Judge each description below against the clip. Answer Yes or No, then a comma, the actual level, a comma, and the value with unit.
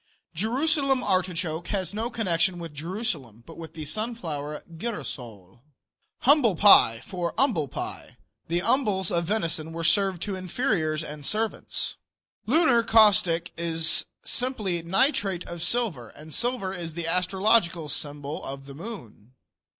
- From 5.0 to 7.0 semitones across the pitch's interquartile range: Yes, wide, 5.6 semitones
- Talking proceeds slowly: Yes, slow, 130 wpm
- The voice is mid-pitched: Yes, medium, 175 Hz